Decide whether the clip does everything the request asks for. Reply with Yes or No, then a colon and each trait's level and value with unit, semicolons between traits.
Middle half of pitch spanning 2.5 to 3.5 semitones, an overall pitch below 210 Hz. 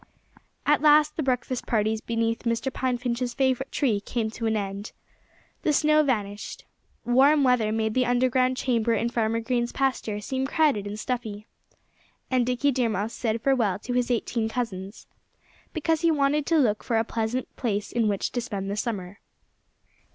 No: average, 3.1 semitones; high, 240 Hz